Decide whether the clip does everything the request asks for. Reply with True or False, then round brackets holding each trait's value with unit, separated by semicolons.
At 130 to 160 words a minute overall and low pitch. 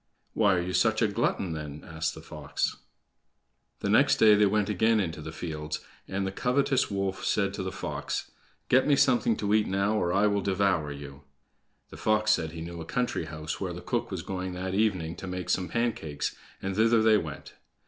False (205 wpm; 95 Hz)